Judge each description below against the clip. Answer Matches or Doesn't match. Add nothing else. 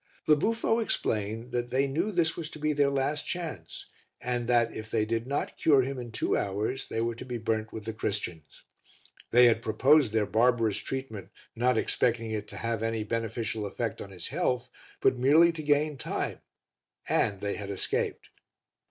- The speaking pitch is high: Doesn't match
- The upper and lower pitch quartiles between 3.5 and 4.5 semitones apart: Matches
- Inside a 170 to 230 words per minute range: Matches